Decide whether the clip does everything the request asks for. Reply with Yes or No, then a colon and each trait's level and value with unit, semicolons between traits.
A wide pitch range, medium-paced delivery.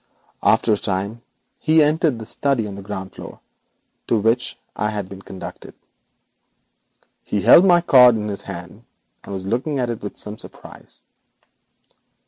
No: average, 4.0 semitones; average, 155 wpm